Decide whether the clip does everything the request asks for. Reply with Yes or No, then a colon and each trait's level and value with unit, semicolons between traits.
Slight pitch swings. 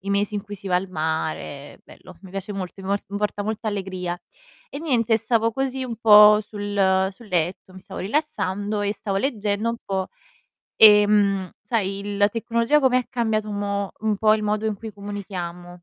Yes: narrow, 2.3 semitones